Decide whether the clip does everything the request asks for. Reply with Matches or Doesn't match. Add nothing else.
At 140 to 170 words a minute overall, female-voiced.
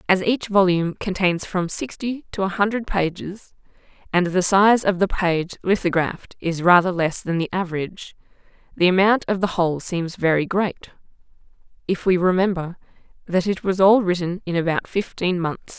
Matches